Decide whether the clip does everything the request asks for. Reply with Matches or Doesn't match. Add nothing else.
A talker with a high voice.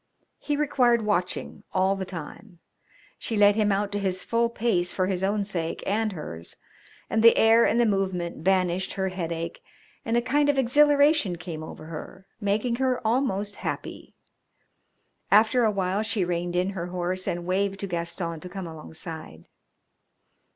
Matches